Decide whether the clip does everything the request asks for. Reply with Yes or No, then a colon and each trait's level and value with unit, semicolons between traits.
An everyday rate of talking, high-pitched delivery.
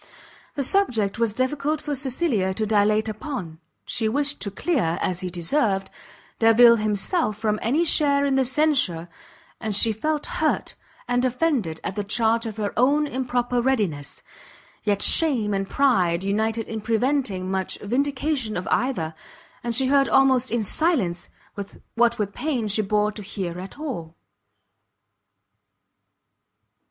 Yes: average, 145 wpm; high, 230 Hz